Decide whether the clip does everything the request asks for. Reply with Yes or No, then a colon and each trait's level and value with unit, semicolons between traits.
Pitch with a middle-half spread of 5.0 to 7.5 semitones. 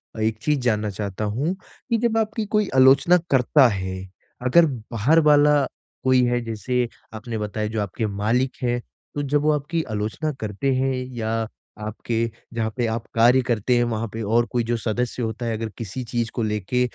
No: average, 3.7 semitones